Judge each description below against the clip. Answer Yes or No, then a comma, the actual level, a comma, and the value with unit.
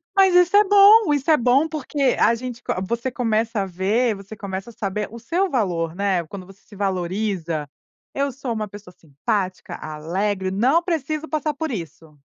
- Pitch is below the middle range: No, high, 220 Hz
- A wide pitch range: Yes, wide, 6.8 semitones